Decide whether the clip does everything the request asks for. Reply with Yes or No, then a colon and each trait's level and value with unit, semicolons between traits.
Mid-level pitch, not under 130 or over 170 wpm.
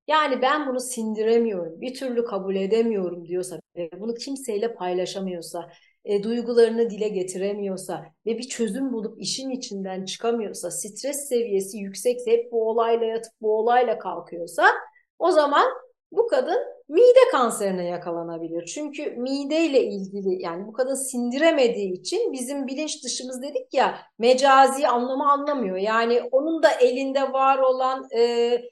No: high, 235 Hz; average, 135 wpm